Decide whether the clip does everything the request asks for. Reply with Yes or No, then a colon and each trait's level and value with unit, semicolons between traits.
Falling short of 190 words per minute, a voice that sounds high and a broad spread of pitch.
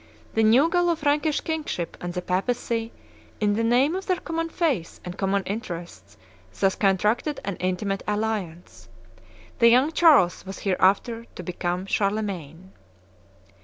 Yes: slow, 135 wpm; high, 210 Hz; wide, 6.4 semitones